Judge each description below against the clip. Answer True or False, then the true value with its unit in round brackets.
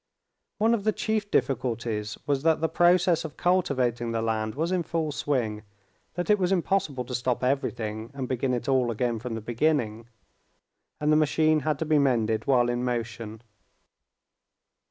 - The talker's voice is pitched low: True (130 Hz)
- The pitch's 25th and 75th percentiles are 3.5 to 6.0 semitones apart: True (5.4 semitones)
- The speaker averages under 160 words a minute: False (170 wpm)